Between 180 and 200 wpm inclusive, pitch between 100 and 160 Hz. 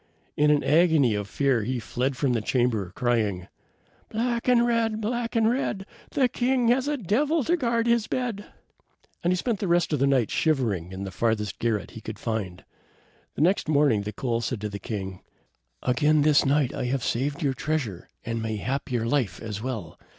Yes: average, 195 wpm; low, 135 Hz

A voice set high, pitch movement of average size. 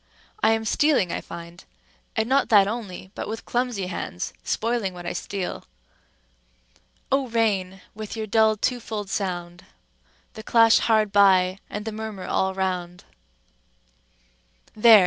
Yes: high, 210 Hz; average, 3.2 semitones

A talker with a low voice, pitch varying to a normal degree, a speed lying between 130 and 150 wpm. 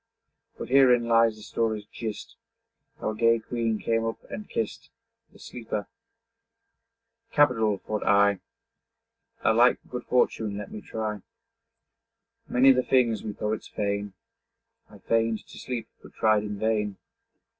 No: low, 110 Hz; narrow, 1.8 semitones; slow, 135 wpm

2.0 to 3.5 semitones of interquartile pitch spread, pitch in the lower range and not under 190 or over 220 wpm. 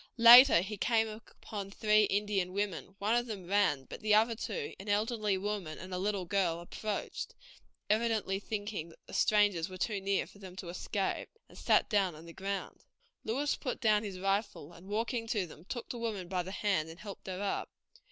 No: narrow, 2.6 semitones; high, 205 Hz; average, 200 wpm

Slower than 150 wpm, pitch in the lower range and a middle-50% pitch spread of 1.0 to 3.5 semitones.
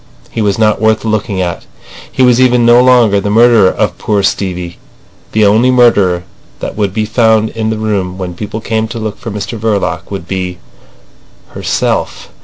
No: average, 175 wpm; low, 105 Hz; average, 2.9 semitones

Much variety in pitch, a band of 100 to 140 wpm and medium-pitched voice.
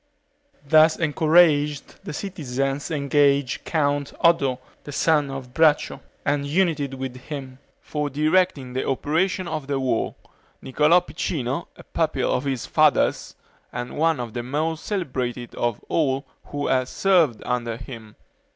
No: average, 3.4 semitones; slow, 135 wpm; medium, 145 Hz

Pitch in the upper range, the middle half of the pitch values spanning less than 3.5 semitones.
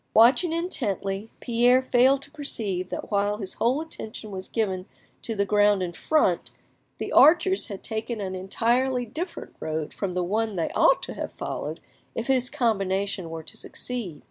No: high, 220 Hz; average, 4.8 semitones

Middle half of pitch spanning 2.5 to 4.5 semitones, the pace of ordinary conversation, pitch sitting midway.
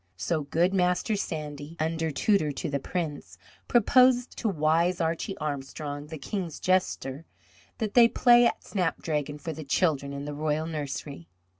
Yes: average, 4.1 semitones; average, 150 wpm; medium, 160 Hz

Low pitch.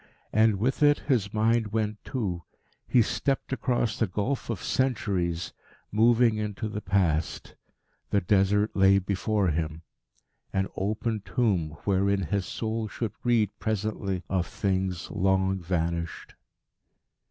Yes: low, 100 Hz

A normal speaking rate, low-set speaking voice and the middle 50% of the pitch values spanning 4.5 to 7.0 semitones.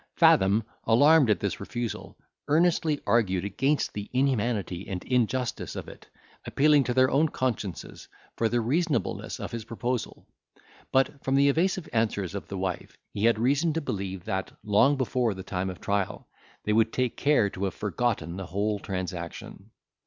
Yes: average, 165 wpm; low, 115 Hz; wide, 5.4 semitones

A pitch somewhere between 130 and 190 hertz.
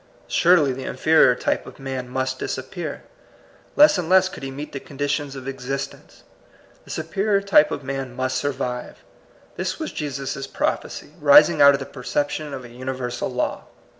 Yes: low, 135 Hz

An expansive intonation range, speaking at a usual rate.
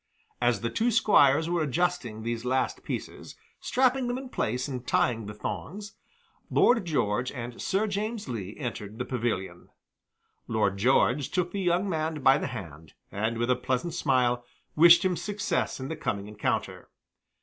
Yes: wide, 7.4 semitones; average, 160 wpm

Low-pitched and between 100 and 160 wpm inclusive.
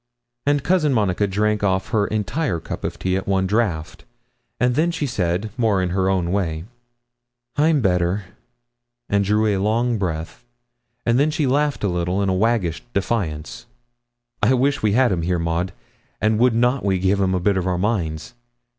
No: low, 100 Hz; average, 180 wpm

